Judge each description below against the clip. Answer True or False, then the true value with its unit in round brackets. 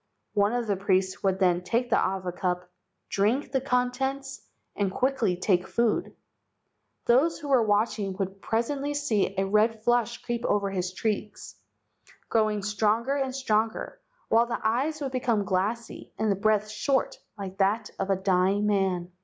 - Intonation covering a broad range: False (3.9 semitones)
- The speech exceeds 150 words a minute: True (160 wpm)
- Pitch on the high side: True (215 Hz)